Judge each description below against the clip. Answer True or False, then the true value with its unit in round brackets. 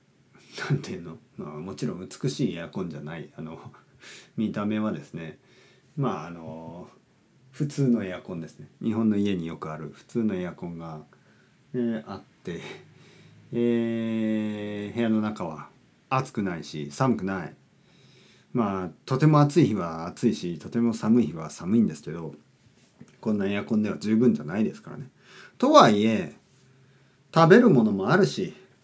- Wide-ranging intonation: False (4.4 semitones)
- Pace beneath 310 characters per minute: True (300 characters per minute)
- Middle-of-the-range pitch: False (110 Hz)